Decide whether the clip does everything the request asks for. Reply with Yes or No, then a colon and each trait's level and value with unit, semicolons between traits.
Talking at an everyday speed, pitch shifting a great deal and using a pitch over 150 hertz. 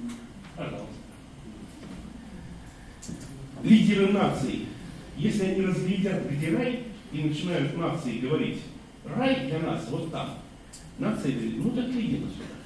No: slow, 100 wpm; wide, 6.6 semitones; high, 190 Hz